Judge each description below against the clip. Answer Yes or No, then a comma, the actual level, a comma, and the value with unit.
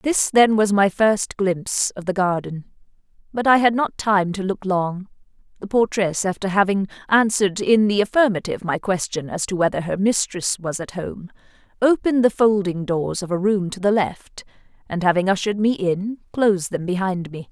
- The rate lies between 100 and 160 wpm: No, average, 185 wpm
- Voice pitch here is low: No, high, 195 Hz